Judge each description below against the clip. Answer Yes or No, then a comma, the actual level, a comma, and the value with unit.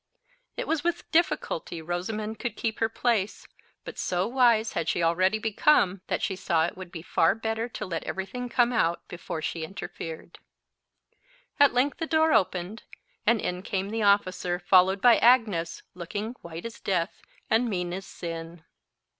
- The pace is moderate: Yes, average, 170 wpm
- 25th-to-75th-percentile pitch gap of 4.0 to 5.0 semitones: Yes, average, 4.7 semitones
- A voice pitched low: No, high, 195 Hz